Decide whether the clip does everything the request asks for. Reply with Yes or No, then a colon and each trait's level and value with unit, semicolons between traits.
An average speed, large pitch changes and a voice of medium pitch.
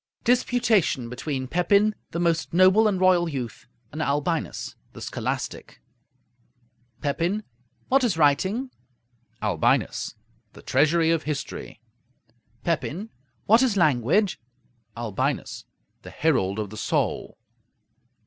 No: slow, 105 wpm; wide, 6.3 semitones; medium, 165 Hz